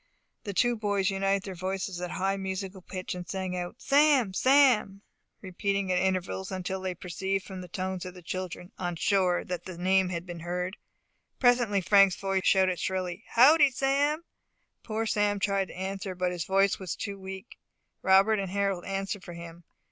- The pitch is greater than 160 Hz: Yes, high, 190 Hz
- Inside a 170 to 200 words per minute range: Yes, average, 185 wpm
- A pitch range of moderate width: No, narrow, 1.7 semitones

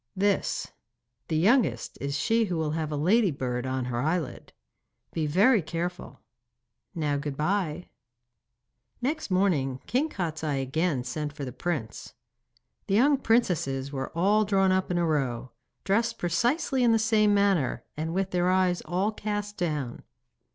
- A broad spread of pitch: Yes, wide, 6.0 semitones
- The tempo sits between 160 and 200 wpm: No, average, 150 wpm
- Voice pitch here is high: No, medium, 175 Hz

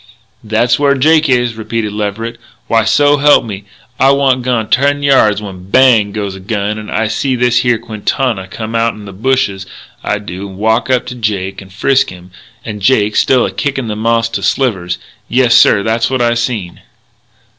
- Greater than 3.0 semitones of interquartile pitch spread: Yes, average, 3.6 semitones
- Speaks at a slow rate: No, average, 185 wpm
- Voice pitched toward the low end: Yes, low, 115 Hz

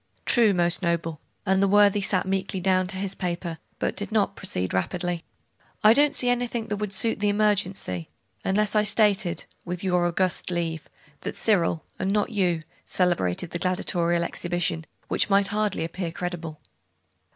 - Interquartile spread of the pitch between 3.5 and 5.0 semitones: No, average, 3.1 semitones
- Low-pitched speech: No, medium, 185 Hz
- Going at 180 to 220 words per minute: No, average, 160 wpm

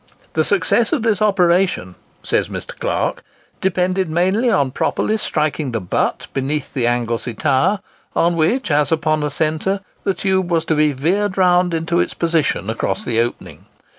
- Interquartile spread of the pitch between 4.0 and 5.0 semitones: Yes, average, 4.6 semitones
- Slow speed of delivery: No, average, 165 wpm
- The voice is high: No, medium, 165 Hz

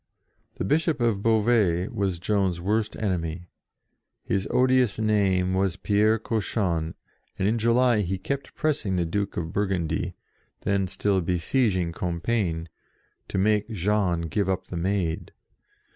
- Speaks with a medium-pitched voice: No, low, 100 Hz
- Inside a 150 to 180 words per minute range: No, slow, 135 wpm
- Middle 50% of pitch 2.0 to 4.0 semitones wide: Yes, average, 3.6 semitones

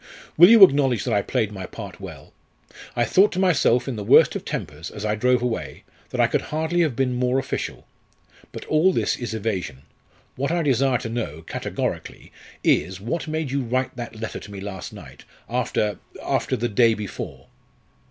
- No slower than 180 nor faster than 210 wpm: Yes, average, 190 wpm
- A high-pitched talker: No, low, 125 Hz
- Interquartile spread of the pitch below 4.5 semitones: No, average, 4.8 semitones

